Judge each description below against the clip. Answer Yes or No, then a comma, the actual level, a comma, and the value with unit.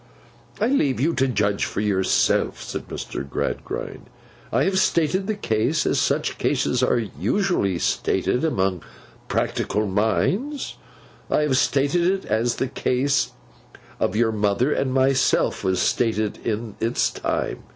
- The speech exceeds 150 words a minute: No, average, 140 wpm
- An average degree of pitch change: No, wide, 6.2 semitones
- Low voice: Yes, low, 125 Hz